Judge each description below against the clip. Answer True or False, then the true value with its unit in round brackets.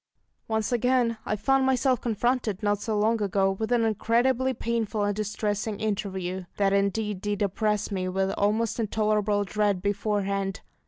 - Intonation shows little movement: True (2.3 semitones)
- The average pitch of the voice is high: True (210 Hz)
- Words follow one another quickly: False (150 wpm)